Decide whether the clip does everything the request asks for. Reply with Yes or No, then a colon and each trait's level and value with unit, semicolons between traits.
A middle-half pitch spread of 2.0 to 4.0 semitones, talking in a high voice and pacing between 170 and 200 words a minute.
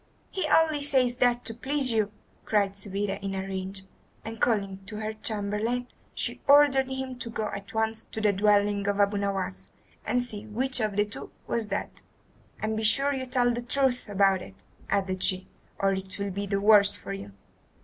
Yes: average, 3.7 semitones; high, 210 Hz; average, 190 wpm